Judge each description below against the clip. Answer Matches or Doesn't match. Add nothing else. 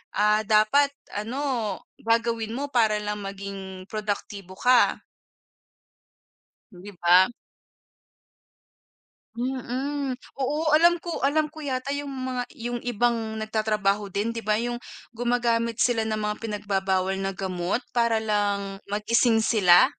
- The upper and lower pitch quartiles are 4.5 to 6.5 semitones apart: Doesn't match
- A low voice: Doesn't match